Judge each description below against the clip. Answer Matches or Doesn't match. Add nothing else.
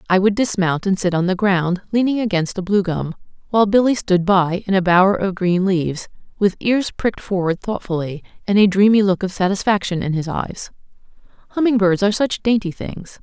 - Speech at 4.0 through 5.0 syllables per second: Doesn't match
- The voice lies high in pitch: Matches